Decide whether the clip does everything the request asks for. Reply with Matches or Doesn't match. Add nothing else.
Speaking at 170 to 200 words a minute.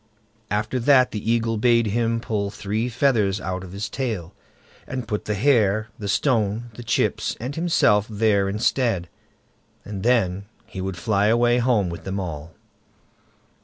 Doesn't match